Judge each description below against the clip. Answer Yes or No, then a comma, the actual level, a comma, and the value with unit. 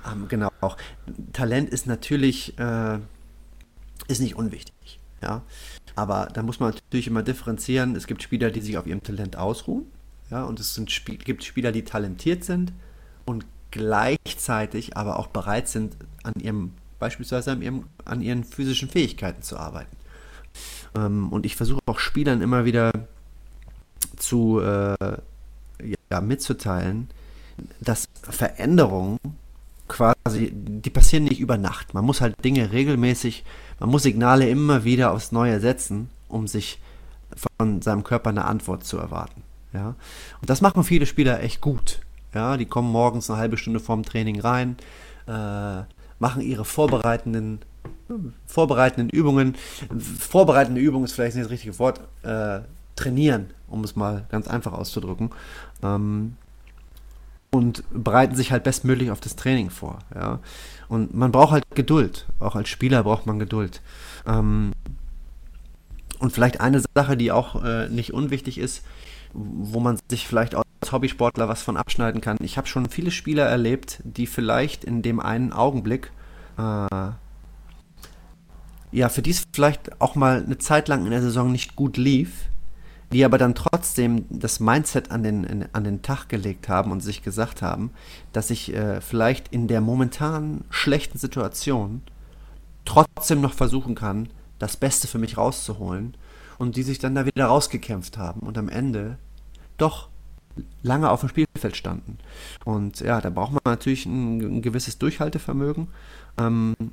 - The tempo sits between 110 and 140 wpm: No, average, 150 wpm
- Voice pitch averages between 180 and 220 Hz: No, low, 115 Hz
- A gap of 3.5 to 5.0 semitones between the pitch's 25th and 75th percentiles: Yes, average, 3.8 semitones